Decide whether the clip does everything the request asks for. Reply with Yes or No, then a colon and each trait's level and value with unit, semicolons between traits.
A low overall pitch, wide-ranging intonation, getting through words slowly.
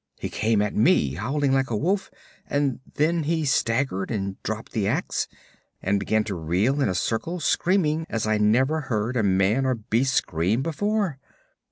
No: low, 125 Hz; wide, 6.2 semitones; average, 175 wpm